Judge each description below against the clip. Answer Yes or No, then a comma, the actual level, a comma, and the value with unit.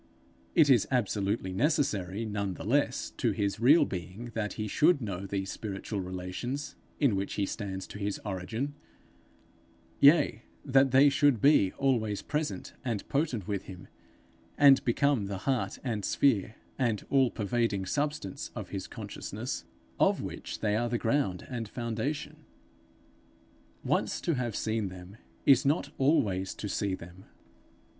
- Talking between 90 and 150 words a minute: Yes, average, 145 wpm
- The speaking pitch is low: Yes, low, 110 Hz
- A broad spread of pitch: Yes, wide, 5.7 semitones